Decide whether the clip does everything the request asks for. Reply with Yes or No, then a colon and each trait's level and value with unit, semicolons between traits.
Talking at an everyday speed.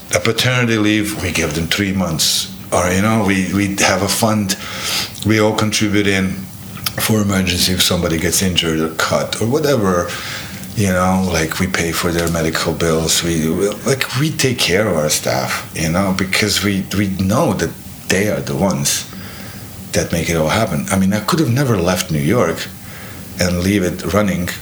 Yes: average, 190 wpm